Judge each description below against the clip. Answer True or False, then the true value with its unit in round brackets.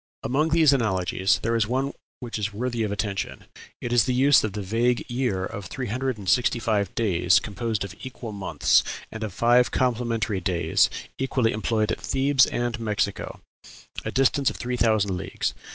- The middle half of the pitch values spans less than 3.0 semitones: False (3.6 semitones)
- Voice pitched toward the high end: False (115 Hz)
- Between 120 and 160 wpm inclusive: False (180 wpm)